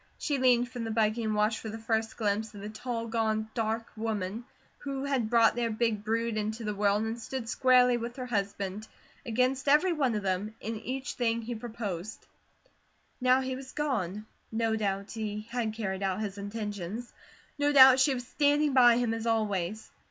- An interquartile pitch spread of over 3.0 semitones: No, narrow, 2.6 semitones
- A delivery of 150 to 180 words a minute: No, average, 190 wpm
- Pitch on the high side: Yes, high, 225 Hz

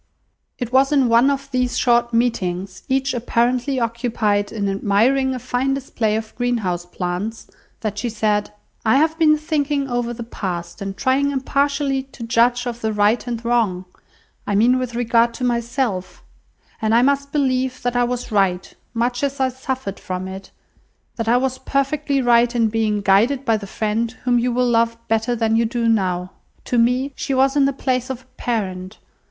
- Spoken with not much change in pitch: No, average, 3.2 semitones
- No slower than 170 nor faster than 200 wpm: Yes, average, 180 wpm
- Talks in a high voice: Yes, high, 240 Hz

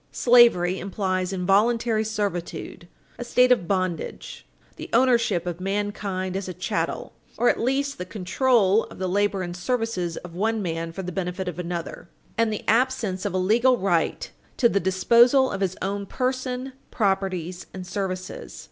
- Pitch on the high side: Yes, high, 195 Hz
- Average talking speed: Yes, average, 160 wpm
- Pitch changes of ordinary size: Yes, average, 4.3 semitones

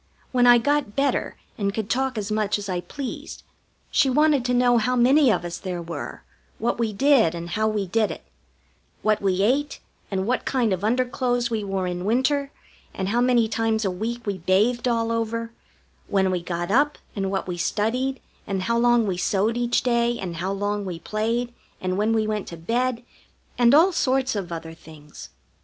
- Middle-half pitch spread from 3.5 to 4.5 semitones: Yes, average, 4.2 semitones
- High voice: Yes, high, 220 Hz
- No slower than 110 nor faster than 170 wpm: No, average, 195 wpm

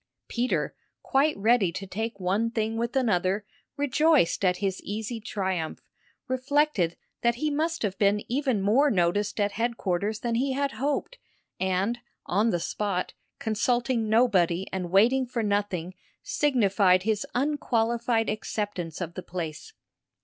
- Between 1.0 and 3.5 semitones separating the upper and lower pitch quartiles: No, average, 4.5 semitones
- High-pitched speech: Yes, high, 220 Hz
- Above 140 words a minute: No, slow, 135 wpm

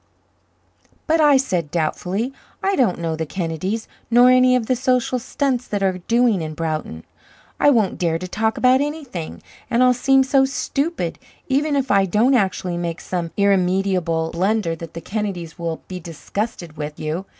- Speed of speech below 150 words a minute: No, average, 170 wpm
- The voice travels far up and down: Yes, wide, 7.0 semitones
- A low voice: No, high, 200 Hz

